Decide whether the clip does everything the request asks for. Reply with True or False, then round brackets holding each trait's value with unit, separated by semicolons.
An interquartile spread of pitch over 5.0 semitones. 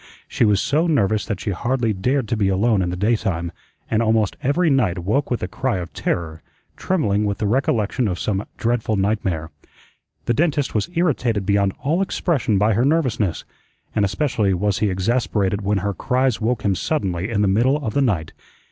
False (4.6 semitones)